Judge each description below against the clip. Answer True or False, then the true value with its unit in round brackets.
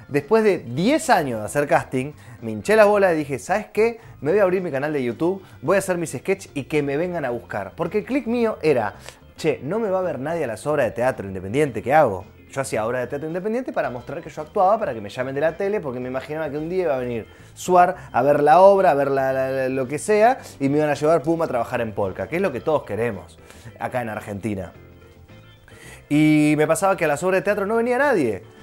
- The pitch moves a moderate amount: False (7.4 semitones)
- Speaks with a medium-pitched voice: True (145 Hz)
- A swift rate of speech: True (260 wpm)